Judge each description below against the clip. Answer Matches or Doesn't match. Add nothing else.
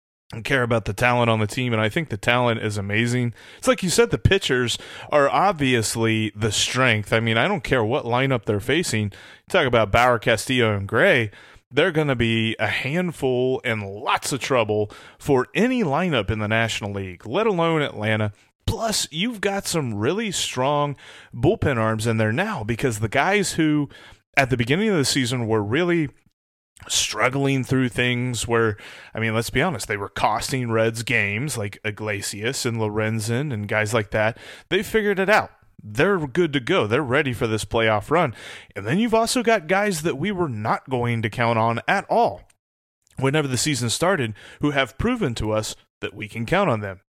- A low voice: Matches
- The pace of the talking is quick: Doesn't match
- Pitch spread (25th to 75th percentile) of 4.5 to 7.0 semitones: Matches